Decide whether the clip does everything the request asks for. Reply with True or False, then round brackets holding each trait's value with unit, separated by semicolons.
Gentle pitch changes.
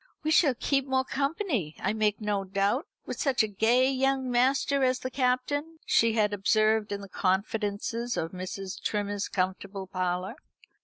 False (4.8 semitones)